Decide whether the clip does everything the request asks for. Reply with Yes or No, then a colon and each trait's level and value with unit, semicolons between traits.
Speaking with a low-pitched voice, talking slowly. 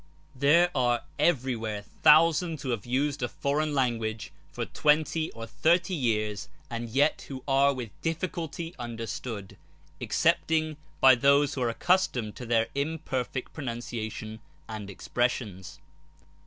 Yes: low, 130 Hz; slow, 120 wpm